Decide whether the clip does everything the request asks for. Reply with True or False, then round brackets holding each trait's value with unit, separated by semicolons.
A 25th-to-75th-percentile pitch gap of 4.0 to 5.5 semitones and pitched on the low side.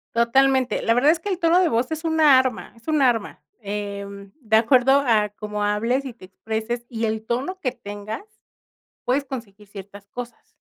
False (4.4 semitones; 235 Hz)